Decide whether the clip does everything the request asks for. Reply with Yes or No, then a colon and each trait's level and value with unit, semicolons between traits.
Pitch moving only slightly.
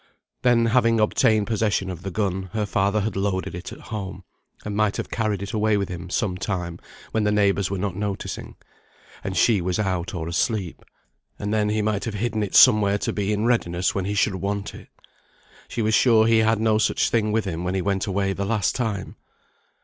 Yes: narrow, 2.2 semitones